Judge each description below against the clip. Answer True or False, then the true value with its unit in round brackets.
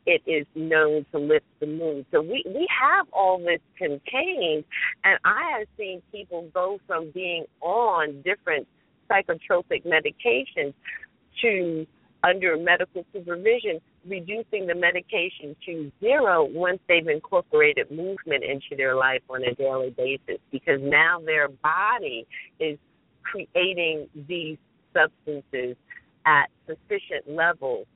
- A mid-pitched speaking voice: True (175 Hz)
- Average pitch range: False (6.7 semitones)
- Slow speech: True (120 wpm)